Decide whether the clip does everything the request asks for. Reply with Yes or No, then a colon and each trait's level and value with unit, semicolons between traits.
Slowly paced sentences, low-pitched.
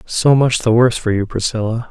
No: fast, 220 wpm; low, 115 Hz